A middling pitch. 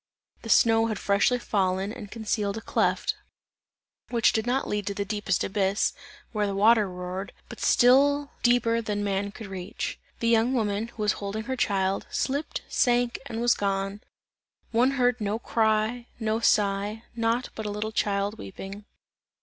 No: high, 215 Hz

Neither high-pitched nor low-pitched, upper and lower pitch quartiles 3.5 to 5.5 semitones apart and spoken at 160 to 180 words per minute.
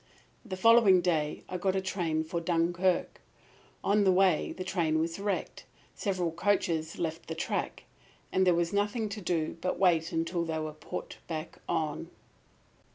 No: medium, 175 Hz; narrow, 2.6 semitones; average, 165 wpm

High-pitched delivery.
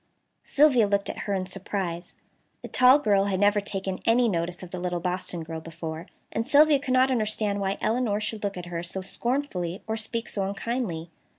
Yes: high, 200 Hz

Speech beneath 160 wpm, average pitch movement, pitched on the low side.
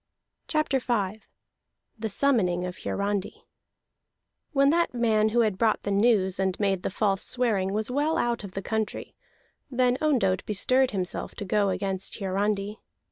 No: average, 150 wpm; average, 3.9 semitones; high, 210 Hz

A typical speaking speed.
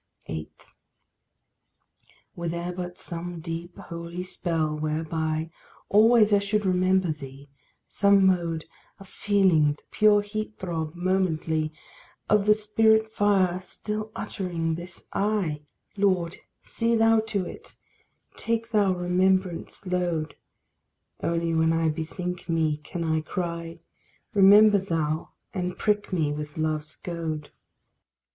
No: slow, 120 wpm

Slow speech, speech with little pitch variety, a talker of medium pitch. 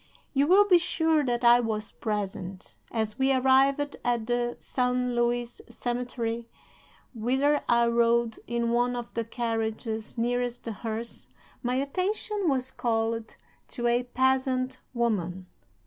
No: slow, 130 wpm; narrow, 2.2 semitones; high, 240 Hz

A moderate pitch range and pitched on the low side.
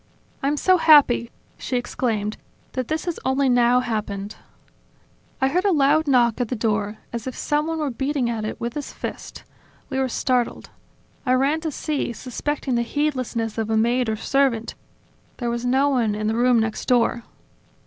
No: average, 3.4 semitones; very high, 250 Hz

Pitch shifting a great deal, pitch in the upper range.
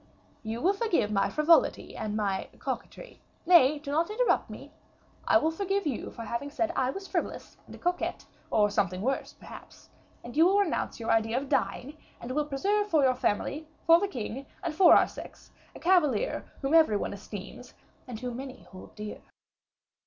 Yes: wide, 7.0 semitones; very high, 280 Hz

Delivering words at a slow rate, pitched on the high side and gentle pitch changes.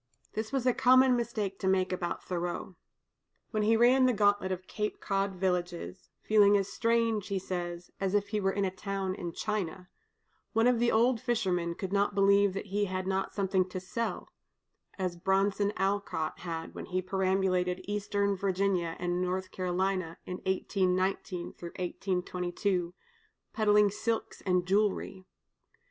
No: average, 155 wpm; high, 195 Hz; narrow, 2.2 semitones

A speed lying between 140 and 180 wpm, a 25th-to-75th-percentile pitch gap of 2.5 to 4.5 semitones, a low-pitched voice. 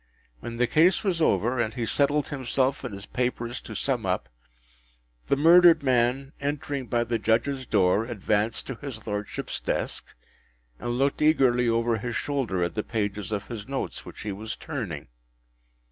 Yes: average, 165 wpm; average, 4.1 semitones; low, 120 Hz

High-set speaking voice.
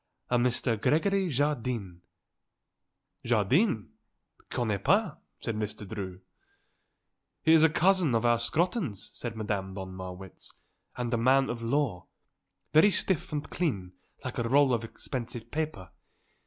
No: low, 120 Hz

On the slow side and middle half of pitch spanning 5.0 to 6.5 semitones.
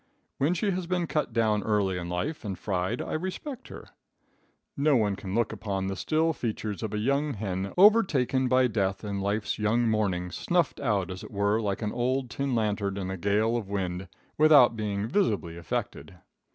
No: average, 190 wpm; wide, 5.6 semitones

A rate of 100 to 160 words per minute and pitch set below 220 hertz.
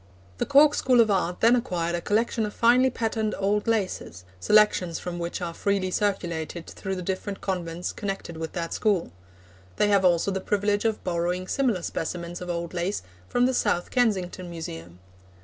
No: average, 175 wpm; high, 190 Hz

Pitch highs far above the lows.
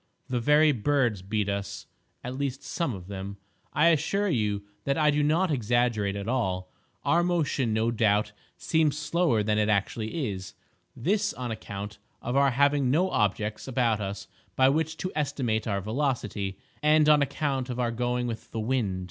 Yes: wide, 5.7 semitones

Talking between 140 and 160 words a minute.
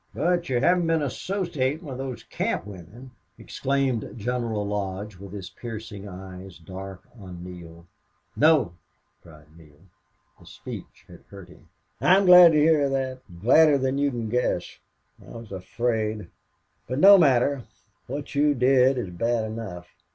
Yes: average, 150 wpm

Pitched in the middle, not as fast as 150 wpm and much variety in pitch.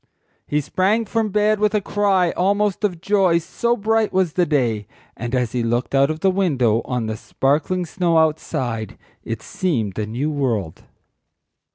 No: medium, 165 Hz; average, 170 wpm; wide, 8.0 semitones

